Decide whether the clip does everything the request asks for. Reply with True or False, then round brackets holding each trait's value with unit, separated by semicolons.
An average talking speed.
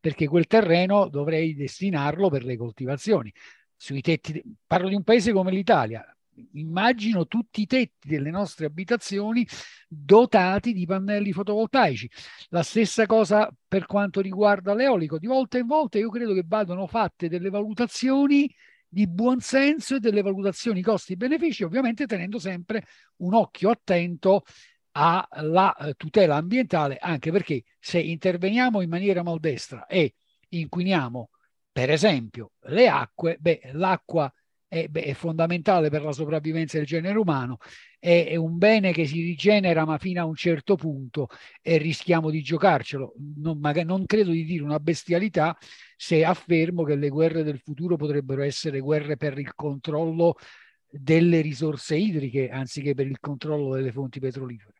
True (145 wpm)